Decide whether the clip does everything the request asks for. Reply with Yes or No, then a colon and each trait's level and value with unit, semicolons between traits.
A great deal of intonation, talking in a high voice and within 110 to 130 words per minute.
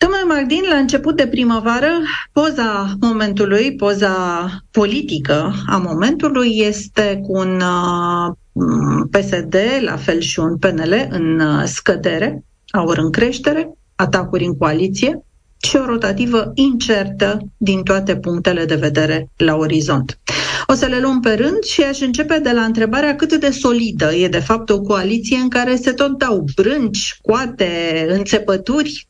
No: wide, 6.8 semitones; high, 210 Hz; average, 140 wpm